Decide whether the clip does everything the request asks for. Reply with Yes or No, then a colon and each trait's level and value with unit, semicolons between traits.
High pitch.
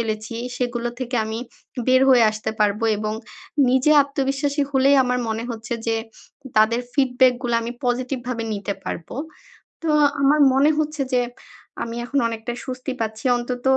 Yes: high, 245 Hz